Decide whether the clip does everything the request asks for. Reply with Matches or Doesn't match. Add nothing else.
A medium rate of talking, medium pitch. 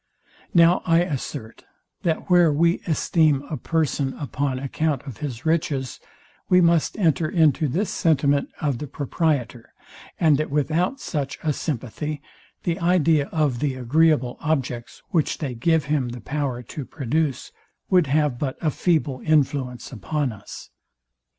Matches